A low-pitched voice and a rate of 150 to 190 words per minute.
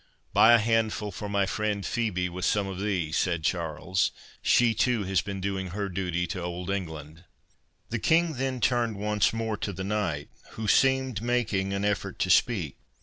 Yes: low, 100 Hz; average, 180 wpm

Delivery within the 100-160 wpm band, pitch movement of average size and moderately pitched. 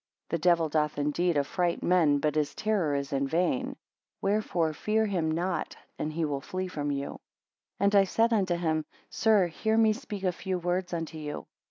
No: average, 185 wpm; average, 4.0 semitones; medium, 170 Hz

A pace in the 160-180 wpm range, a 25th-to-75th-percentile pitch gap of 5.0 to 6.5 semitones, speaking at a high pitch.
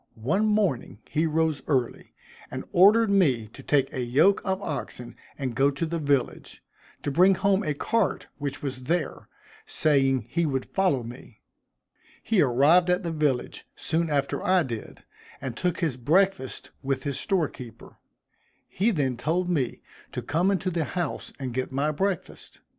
No: average, 165 wpm; wide, 5.5 semitones; medium, 150 Hz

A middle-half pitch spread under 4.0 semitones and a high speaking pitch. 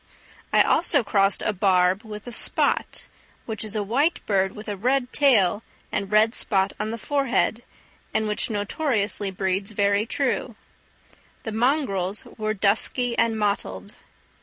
Yes: average, 3.0 semitones; high, 215 Hz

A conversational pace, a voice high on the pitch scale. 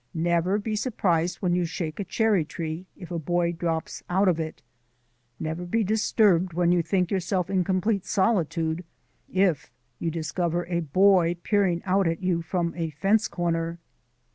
No: average, 165 wpm; medium, 175 Hz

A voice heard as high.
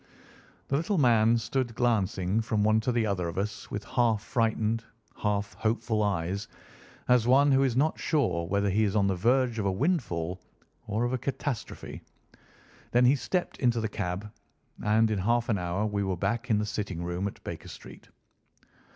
No: low, 110 Hz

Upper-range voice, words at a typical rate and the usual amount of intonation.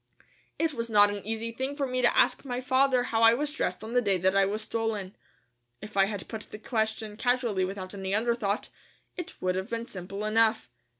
No: high, 220 Hz; fast, 215 wpm; average, 3.4 semitones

